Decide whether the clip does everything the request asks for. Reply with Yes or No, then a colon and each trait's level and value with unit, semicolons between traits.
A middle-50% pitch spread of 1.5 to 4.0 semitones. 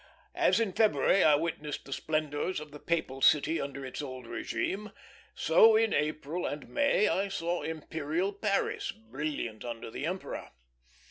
No: average, 5.3 semitones